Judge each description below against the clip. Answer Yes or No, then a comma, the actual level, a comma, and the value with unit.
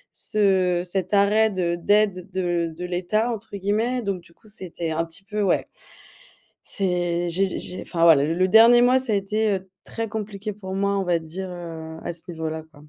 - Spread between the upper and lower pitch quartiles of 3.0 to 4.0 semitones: Yes, average, 3.3 semitones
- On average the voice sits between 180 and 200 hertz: Yes, high, 190 Hz